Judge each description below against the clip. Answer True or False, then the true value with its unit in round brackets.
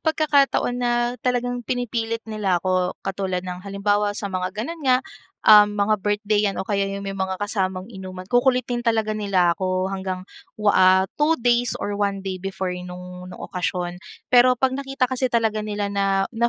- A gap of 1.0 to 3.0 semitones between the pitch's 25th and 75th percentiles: False (4.2 semitones)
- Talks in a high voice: True (205 Hz)